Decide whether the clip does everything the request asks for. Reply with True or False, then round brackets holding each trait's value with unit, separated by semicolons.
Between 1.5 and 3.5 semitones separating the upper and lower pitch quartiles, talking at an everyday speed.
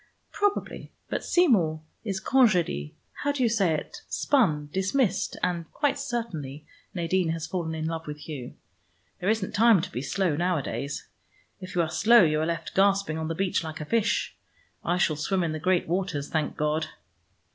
False (4.2 semitones; 180 wpm)